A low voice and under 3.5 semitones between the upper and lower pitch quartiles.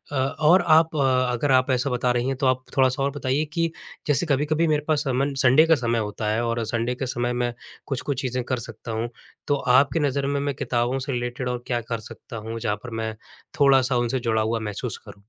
Yes: low, 130 Hz; average, 2.9 semitones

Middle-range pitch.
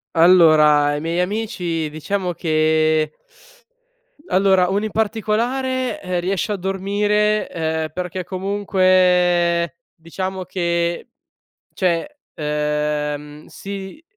Yes: medium, 180 Hz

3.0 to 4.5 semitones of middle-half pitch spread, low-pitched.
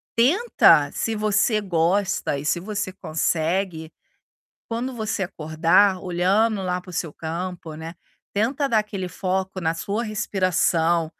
No: average, 4.1 semitones; medium, 185 Hz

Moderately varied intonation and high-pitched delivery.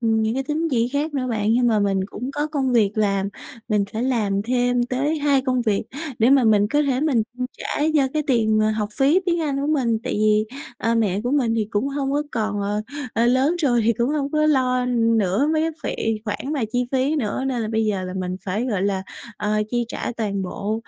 Yes: average, 4.2 semitones; high, 240 Hz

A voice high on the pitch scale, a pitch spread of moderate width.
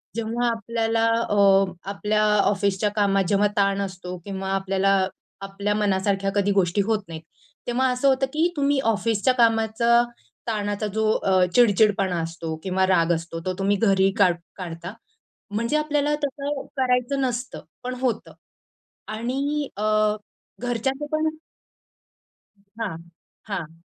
Yes: high, 210 Hz; average, 3.9 semitones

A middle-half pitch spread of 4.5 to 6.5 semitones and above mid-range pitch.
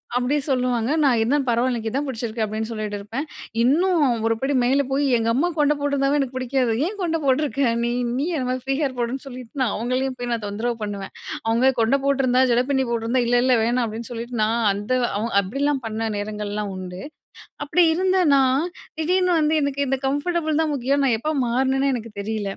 No: average, 3.7 semitones; very high, 255 Hz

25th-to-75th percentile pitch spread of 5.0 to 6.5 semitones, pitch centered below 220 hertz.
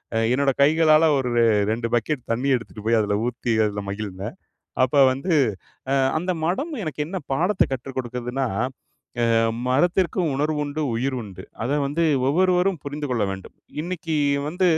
Yes: wide, 5.4 semitones; medium, 140 Hz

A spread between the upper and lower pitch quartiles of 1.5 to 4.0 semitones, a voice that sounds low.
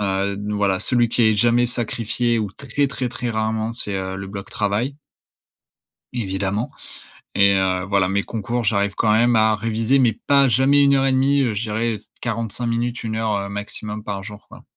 Yes: average, 3.1 semitones; low, 110 Hz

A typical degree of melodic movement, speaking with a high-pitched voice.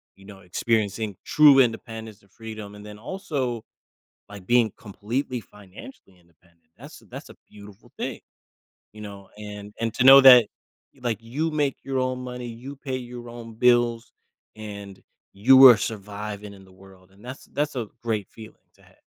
No: average, 3.6 semitones; low, 110 Hz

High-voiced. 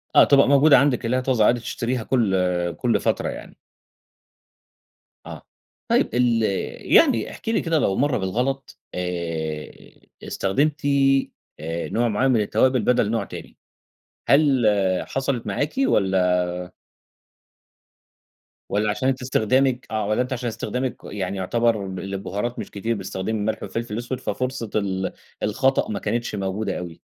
No: low, 115 Hz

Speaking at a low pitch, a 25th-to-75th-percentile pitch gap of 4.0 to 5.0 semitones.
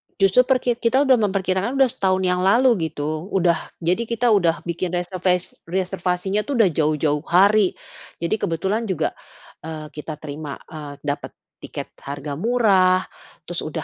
No: medium, 185 Hz; average, 4.6 semitones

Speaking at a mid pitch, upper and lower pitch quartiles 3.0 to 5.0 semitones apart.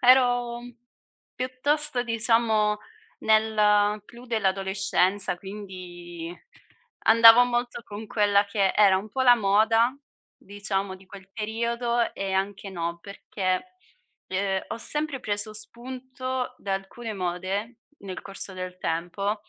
No: high, 210 Hz; average, 3.6 semitones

